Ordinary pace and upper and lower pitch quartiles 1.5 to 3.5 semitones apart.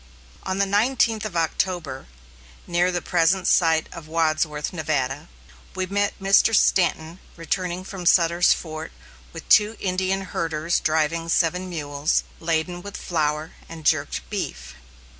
No: slow, 130 wpm; average, 2.9 semitones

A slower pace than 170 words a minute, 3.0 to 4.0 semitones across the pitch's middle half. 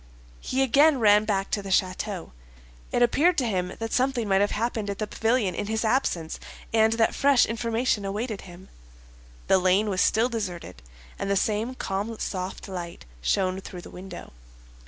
No: average, 175 wpm; average, 3.3 semitones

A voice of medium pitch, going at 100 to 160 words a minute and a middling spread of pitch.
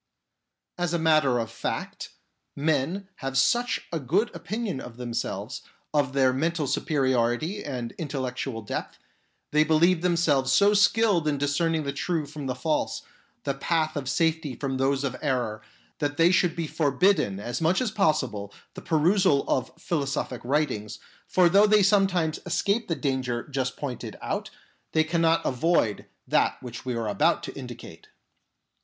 Yes: medium, 150 Hz; average, 155 wpm; average, 4.6 semitones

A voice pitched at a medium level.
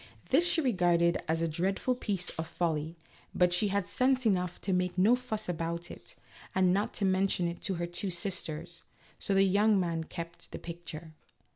Yes: medium, 180 Hz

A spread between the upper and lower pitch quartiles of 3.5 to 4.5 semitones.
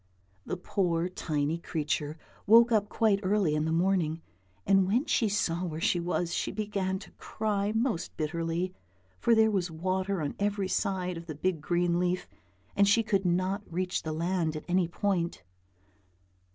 No: average, 3.1 semitones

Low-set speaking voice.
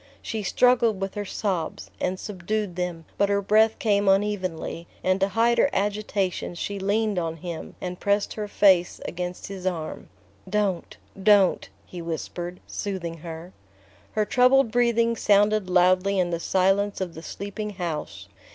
No: high, 195 Hz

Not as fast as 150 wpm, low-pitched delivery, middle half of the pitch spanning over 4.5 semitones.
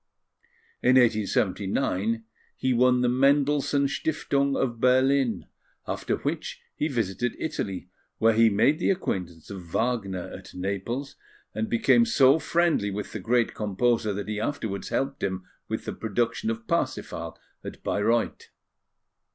Yes: slow, 135 wpm; low, 120 Hz; average, 5.3 semitones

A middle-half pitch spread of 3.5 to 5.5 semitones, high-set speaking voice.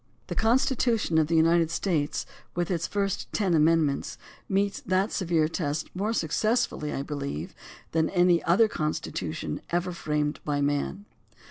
No: average, 4.2 semitones; medium, 165 Hz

